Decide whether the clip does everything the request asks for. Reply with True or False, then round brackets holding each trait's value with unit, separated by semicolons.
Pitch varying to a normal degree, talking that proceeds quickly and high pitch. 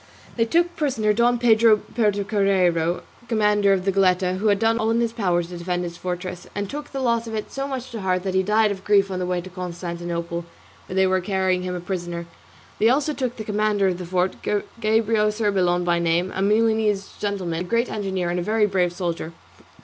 True (3.5 semitones; 215 wpm; 195 Hz)